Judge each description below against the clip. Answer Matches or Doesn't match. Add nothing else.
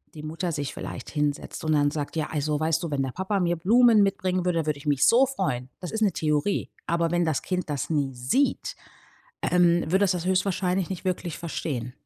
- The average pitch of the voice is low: Doesn't match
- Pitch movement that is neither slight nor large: Matches